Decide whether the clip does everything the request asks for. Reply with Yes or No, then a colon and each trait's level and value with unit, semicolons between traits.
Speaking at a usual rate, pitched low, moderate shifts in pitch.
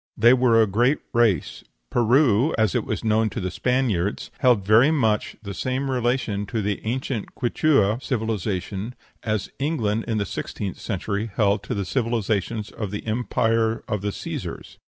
Yes: average, 160 wpm; low, 110 Hz; average, 3.2 semitones